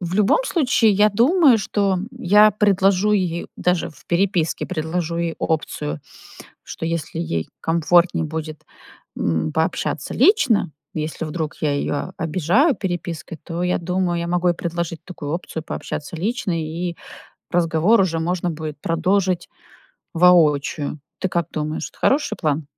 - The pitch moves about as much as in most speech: Yes, average, 3.0 semitones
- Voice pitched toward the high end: No, medium, 170 Hz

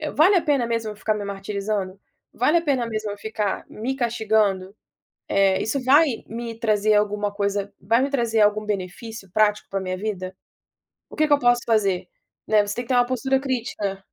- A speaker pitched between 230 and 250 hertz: No, high, 215 Hz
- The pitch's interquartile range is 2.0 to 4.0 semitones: Yes, average, 3.2 semitones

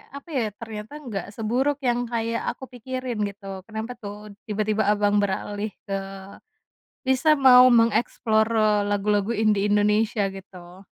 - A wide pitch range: No, narrow, 2.5 semitones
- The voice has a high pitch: Yes, high, 215 Hz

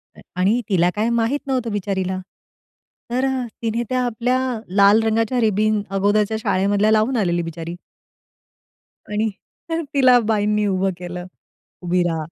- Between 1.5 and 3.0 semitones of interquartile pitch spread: No, average, 3.5 semitones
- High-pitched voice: Yes, high, 210 Hz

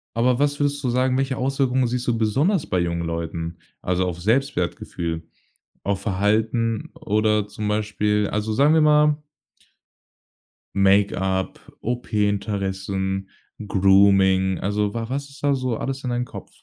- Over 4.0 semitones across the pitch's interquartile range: Yes, average, 5.0 semitones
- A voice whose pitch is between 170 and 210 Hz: No, low, 105 Hz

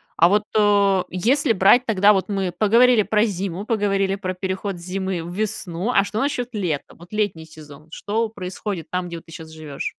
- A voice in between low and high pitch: No, high, 195 Hz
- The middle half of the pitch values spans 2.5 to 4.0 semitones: Yes, average, 3.2 semitones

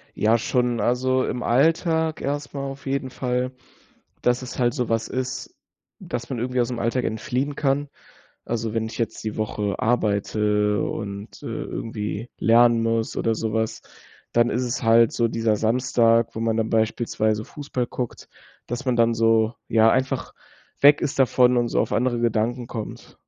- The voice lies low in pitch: Yes, low, 120 Hz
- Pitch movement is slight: Yes, narrow, 2.3 semitones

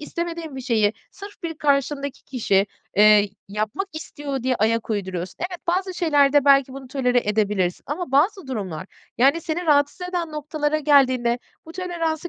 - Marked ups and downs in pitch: Yes, wide, 5.9 semitones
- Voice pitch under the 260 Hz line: No, very high, 280 Hz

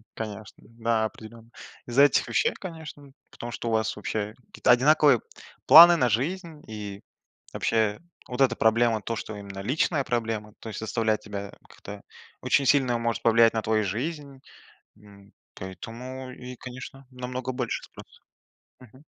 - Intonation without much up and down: No, average, 3.2 semitones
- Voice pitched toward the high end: No, low, 115 Hz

